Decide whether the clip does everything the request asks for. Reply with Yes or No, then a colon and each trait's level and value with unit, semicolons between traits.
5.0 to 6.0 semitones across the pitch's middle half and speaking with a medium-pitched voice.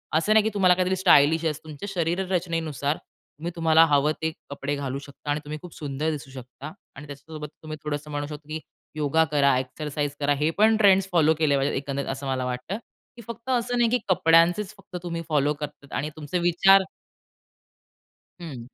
No: average, 3.6 semitones; medium, 155 Hz